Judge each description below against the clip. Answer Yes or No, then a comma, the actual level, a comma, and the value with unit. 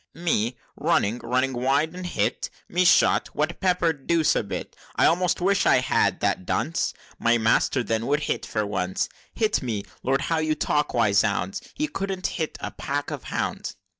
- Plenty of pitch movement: Yes, wide, 6.5 semitones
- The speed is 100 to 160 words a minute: No, average, 180 wpm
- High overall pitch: No, medium, 145 Hz